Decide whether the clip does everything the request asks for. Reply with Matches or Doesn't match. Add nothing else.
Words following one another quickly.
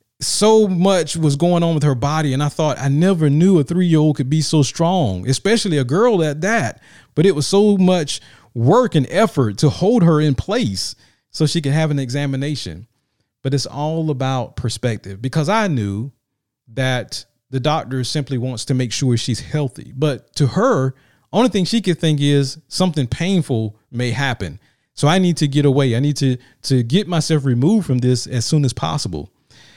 Doesn't match